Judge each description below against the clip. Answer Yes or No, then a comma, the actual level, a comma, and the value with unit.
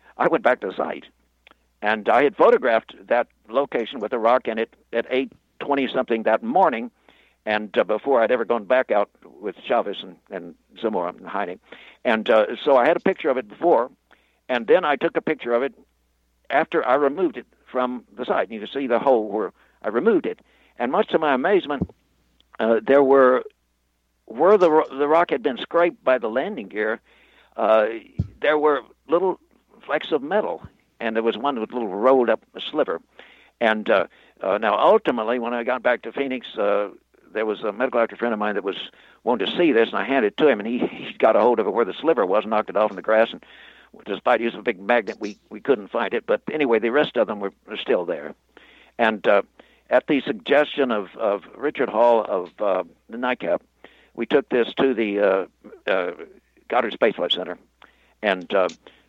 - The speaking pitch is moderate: No, low, 120 Hz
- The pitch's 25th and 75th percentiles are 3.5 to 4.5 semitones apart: Yes, average, 3.9 semitones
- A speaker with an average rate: No, fast, 210 wpm